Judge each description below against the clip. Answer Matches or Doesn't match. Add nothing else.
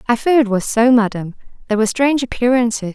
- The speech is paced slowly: Doesn't match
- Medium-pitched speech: Doesn't match